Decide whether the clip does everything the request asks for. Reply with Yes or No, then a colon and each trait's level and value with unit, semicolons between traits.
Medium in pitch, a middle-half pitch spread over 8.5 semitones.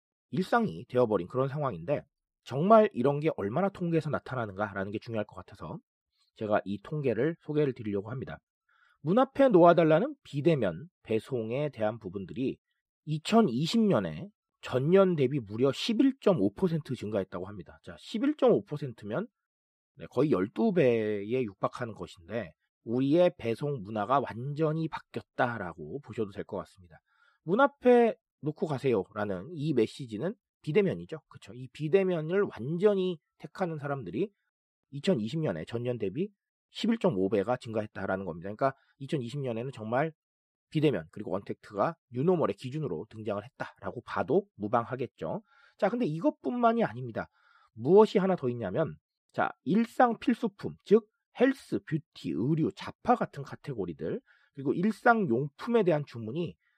Yes: medium, 150 Hz; wide, 8.9 semitones